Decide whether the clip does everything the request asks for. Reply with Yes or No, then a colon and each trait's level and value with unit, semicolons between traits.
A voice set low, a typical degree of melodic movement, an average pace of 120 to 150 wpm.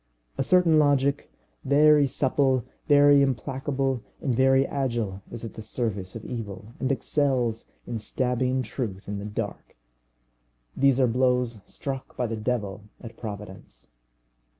Yes: low, 125 Hz; average, 3.7 semitones; slow, 135 wpm